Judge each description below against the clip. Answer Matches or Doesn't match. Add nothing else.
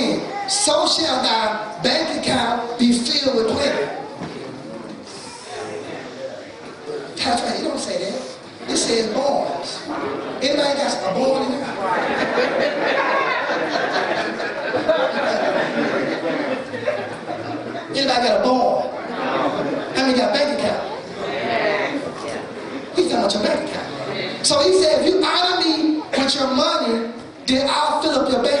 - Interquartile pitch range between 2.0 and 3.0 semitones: Doesn't match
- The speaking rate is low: Matches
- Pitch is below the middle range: Doesn't match